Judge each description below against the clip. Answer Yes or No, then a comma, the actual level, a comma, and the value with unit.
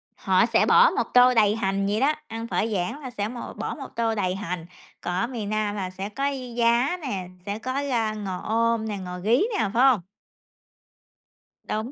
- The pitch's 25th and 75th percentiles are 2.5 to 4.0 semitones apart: Yes, average, 3.3 semitones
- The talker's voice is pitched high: Yes, high, 220 Hz